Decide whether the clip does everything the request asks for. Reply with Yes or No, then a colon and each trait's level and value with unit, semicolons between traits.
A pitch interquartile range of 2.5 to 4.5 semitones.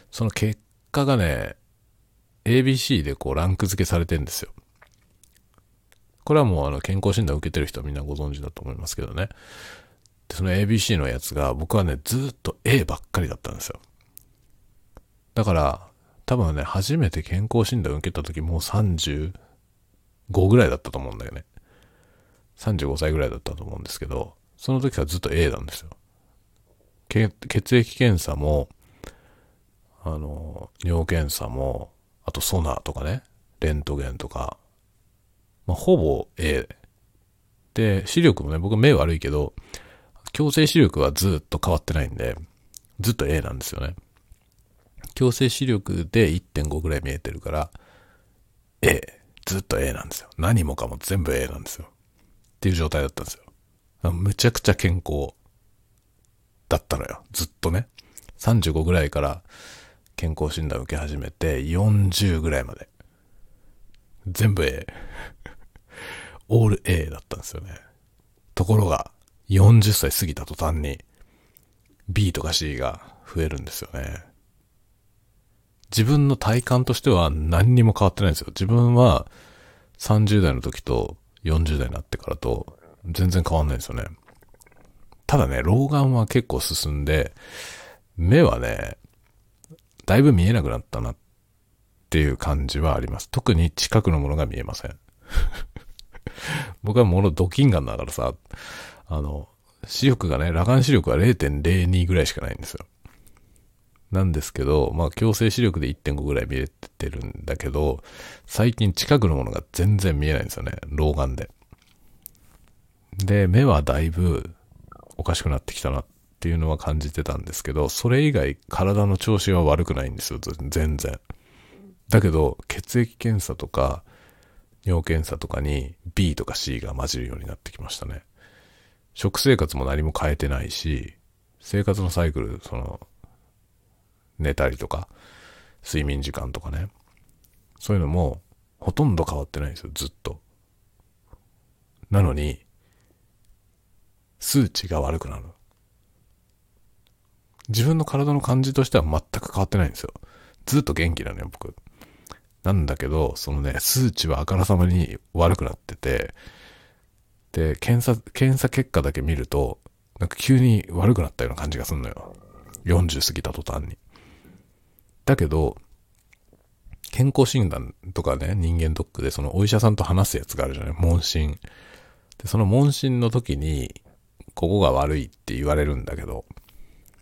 No: wide, 5.5 semitones